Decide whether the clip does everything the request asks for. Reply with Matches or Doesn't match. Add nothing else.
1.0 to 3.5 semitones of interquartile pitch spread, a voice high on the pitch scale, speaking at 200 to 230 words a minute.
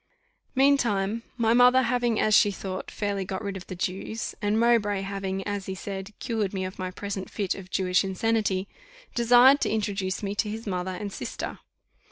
Doesn't match